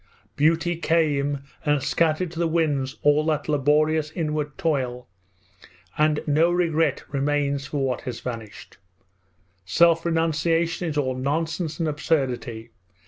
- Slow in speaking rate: Yes, slow, 125 wpm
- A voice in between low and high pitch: Yes, medium, 150 Hz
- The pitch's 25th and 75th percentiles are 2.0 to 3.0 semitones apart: Yes, average, 2.7 semitones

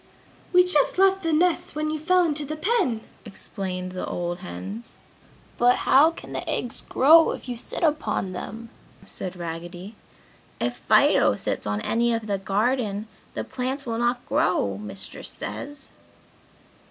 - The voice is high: Yes, high, 235 Hz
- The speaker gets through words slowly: No, average, 155 wpm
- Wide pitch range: Yes, wide, 8.8 semitones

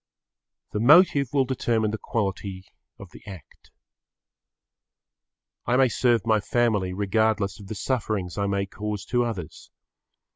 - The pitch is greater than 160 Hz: No, low, 110 Hz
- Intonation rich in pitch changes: No, average, 3.3 semitones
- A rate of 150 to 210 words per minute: No, slow, 135 wpm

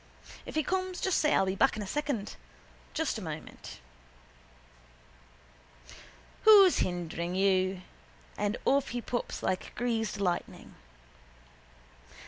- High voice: Yes, high, 220 Hz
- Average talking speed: No, slow, 115 wpm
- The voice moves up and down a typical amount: No, wide, 7.7 semitones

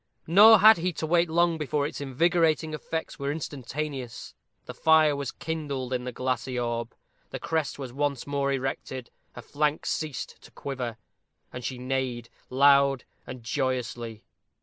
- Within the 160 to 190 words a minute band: No, average, 150 wpm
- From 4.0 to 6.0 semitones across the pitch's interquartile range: No, average, 3.6 semitones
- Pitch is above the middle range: No, medium, 140 Hz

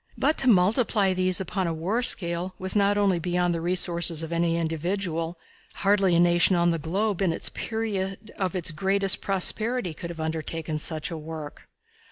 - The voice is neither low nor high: Yes, medium, 180 Hz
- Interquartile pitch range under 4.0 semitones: Yes, average, 2.8 semitones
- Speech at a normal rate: Yes, average, 180 wpm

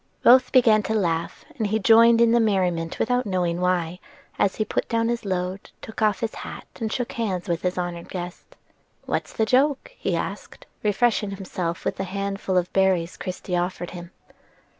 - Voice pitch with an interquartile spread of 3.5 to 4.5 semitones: Yes, average, 3.9 semitones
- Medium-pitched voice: No, high, 195 Hz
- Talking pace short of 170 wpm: No, average, 180 wpm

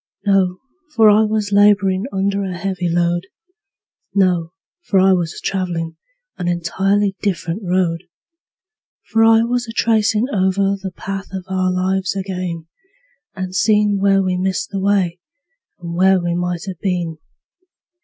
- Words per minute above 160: No, average, 145 wpm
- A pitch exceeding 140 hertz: Yes, high, 190 Hz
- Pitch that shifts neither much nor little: No, narrow, 2.1 semitones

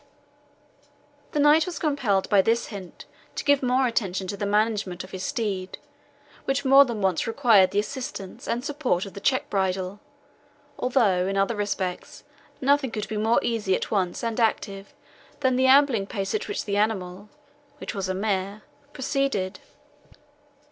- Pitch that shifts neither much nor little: Yes, average, 5.0 semitones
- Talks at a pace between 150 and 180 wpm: Yes, average, 160 wpm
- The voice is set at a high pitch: Yes, high, 210 Hz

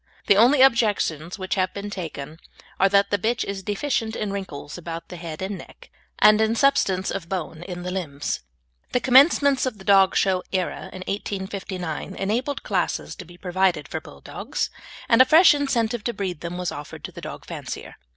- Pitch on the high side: Yes, high, 195 Hz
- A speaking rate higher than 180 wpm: Yes, average, 190 wpm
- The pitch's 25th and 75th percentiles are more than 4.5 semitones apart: No, average, 3.9 semitones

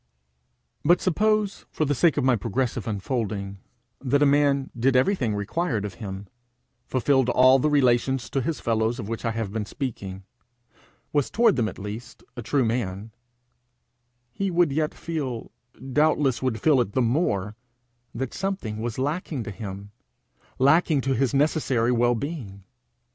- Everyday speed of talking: Yes, average, 155 wpm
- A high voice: No, low, 125 Hz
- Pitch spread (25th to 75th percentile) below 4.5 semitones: No, average, 4.8 semitones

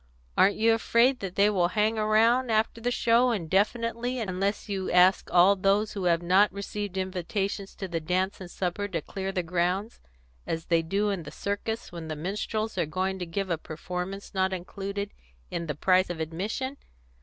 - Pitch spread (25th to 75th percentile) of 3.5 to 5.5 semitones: No, average, 3.0 semitones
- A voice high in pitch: Yes, high, 195 Hz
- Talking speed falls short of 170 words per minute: No, average, 185 wpm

